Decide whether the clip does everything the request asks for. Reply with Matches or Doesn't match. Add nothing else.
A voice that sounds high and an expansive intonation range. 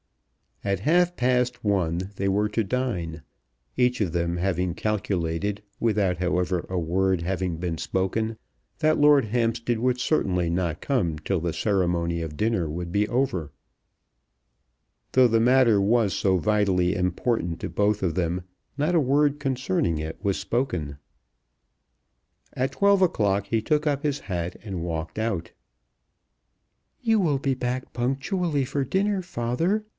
Doesn't match